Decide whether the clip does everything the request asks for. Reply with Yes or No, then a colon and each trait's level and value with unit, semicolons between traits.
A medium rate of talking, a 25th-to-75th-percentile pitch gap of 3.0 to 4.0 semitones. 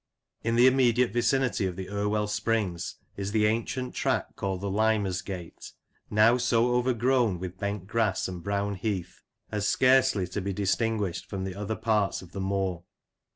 Yes: average, 160 wpm; average, 3.3 semitones